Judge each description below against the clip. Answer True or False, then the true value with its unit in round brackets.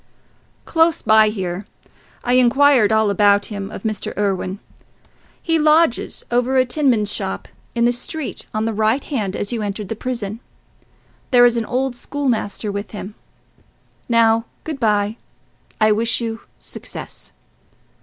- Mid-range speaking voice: False (225 Hz)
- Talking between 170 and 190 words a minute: False (145 wpm)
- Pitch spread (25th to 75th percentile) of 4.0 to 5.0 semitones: False (3.4 semitones)